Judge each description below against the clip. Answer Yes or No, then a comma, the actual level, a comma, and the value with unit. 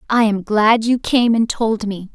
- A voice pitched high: Yes, high, 220 Hz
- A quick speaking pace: Yes, fast, 225 wpm